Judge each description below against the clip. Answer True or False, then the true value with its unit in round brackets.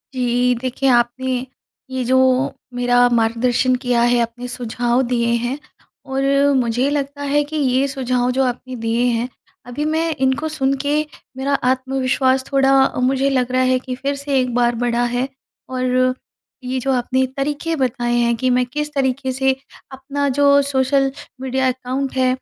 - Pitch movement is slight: True (1.8 semitones)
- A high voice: True (260 Hz)